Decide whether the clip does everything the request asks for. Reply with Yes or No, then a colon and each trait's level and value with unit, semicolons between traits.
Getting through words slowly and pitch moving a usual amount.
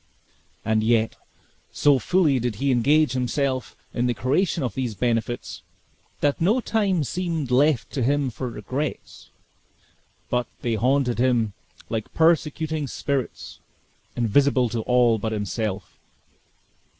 Yes: slow, 125 wpm; average, 3.9 semitones